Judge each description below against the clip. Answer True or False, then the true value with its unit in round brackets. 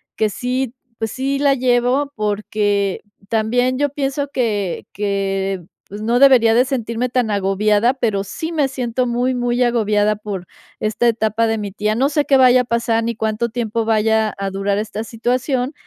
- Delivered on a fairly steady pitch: False (3.2 semitones)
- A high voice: True (230 Hz)